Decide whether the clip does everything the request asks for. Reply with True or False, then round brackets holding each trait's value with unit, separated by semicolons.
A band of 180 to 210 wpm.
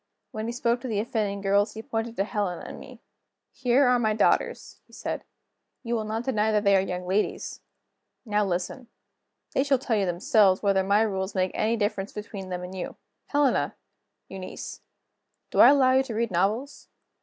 True (190 wpm)